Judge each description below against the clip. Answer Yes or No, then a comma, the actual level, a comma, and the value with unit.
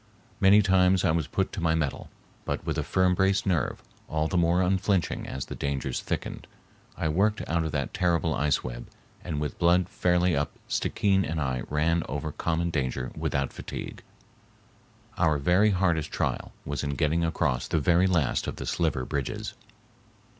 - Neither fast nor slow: Yes, average, 175 wpm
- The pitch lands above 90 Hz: No, very low, 85 Hz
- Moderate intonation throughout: Yes, average, 3.8 semitones